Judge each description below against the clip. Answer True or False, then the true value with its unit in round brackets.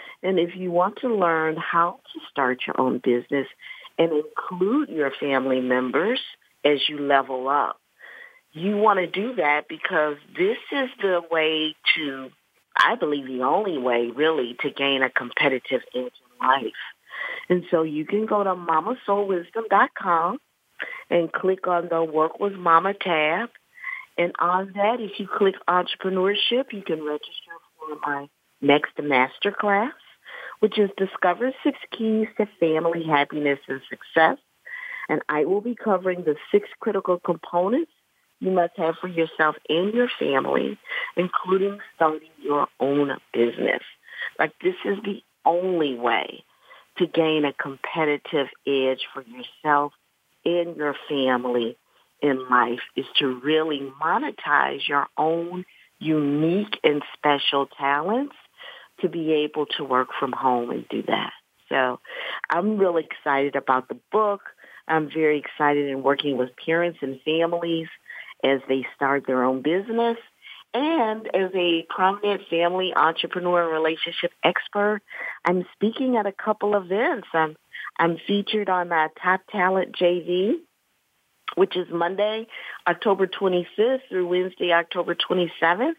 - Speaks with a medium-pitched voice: True (170 Hz)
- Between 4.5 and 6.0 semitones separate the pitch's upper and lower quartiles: True (5.3 semitones)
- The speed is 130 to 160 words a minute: True (135 wpm)